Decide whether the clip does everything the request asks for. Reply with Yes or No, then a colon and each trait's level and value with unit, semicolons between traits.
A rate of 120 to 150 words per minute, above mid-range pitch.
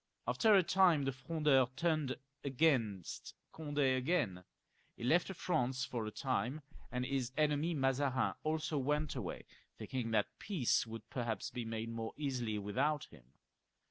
No: average, 140 wpm; low, 135 Hz